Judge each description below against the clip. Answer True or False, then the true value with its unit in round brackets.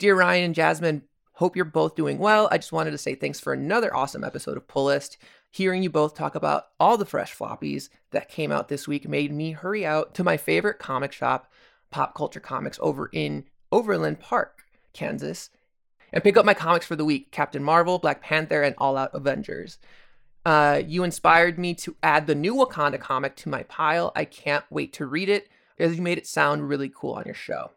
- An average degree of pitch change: True (3.5 semitones)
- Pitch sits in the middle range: True (155 Hz)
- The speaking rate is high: True (210 wpm)